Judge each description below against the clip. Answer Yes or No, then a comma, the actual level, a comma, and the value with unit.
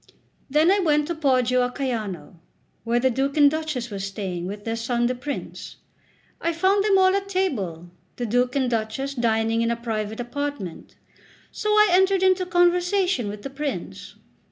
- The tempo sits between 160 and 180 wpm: Yes, average, 175 wpm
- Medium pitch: No, very high, 260 Hz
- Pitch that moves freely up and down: Yes, wide, 7.2 semitones